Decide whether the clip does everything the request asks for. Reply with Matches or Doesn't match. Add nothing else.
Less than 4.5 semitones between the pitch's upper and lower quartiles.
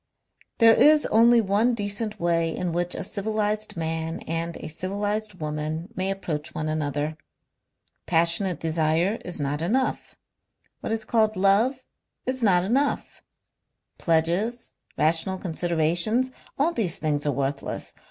Doesn't match